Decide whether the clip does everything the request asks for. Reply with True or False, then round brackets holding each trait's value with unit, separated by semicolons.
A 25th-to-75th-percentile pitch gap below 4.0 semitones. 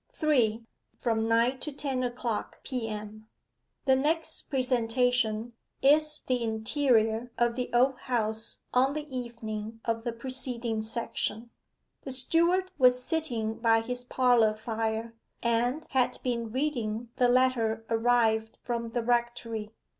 True (2.4 semitones)